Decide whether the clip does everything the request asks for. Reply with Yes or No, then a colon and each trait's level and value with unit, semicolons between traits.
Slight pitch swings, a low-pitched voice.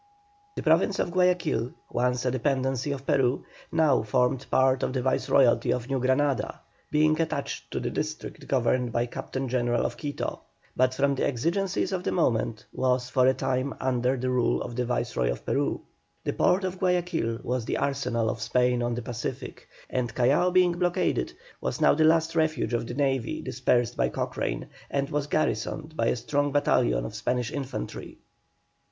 No: average, 3.4 semitones; low, 130 Hz